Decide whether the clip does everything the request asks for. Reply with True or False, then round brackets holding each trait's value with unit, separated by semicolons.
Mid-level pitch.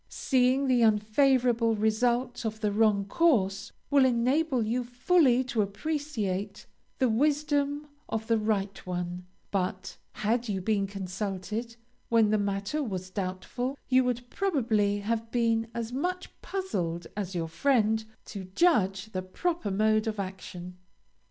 False (220 Hz)